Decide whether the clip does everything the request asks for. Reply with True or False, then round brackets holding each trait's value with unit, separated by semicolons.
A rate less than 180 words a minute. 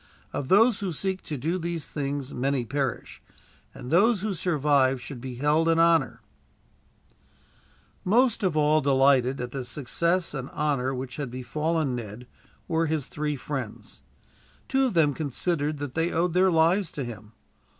True (160 wpm)